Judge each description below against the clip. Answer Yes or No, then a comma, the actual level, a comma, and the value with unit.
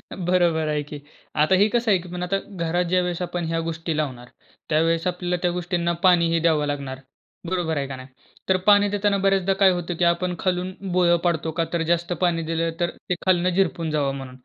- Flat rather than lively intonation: Yes, narrow, 2.1 semitones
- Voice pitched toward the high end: No, medium, 175 Hz